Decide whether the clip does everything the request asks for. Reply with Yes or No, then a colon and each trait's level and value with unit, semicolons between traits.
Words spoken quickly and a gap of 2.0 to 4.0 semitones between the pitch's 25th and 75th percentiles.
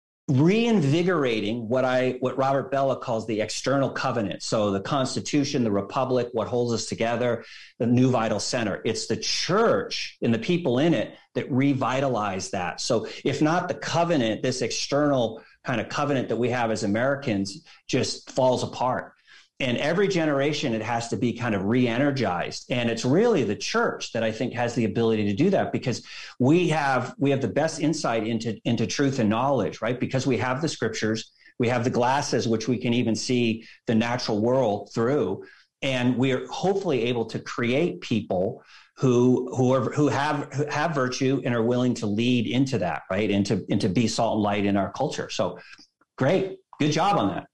No: average, 185 wpm; average, 3.3 semitones